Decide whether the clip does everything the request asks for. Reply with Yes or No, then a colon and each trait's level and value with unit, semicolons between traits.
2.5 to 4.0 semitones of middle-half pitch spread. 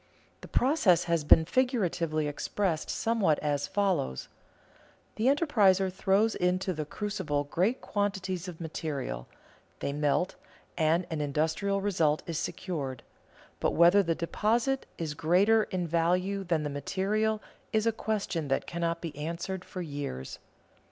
No: average, 4.5 semitones